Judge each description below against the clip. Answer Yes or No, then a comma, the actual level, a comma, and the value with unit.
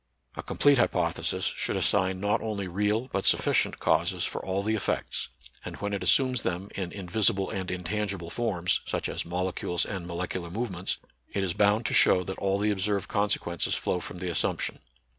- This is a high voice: No, very low, 95 Hz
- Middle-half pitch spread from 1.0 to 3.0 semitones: Yes, narrow, 2.4 semitones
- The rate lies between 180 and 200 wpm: Yes, average, 185 wpm